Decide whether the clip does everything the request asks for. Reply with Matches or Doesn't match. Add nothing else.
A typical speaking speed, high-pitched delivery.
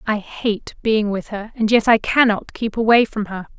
Doesn't match